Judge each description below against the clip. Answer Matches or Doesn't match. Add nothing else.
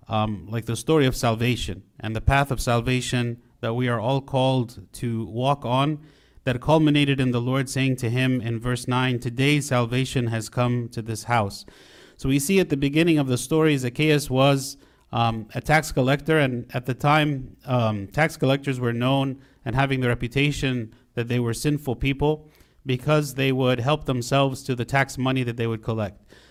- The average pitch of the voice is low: Matches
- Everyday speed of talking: Matches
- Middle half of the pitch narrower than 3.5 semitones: Matches